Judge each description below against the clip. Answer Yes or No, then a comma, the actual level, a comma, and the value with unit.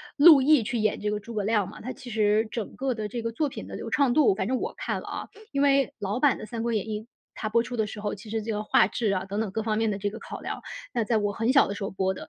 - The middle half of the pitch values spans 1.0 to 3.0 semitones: Yes, narrow, 2.6 semitones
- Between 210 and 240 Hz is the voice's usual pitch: Yes, high, 220 Hz